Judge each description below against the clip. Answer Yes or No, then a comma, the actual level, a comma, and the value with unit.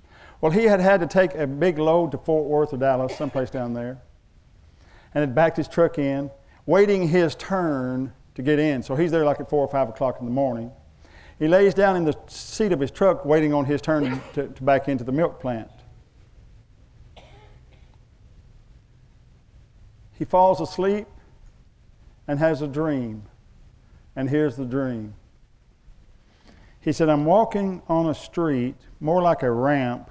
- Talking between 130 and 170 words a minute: Yes, average, 165 wpm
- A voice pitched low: No, medium, 145 Hz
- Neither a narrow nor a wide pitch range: Yes, average, 4.8 semitones